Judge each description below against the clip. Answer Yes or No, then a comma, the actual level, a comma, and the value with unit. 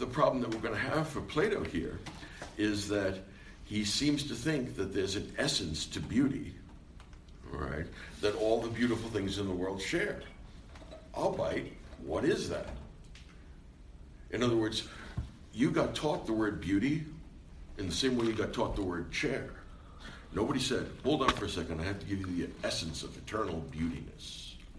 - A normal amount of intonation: No, wide, 5.9 semitones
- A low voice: Yes, very low, 95 Hz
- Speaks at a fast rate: No, average, 175 wpm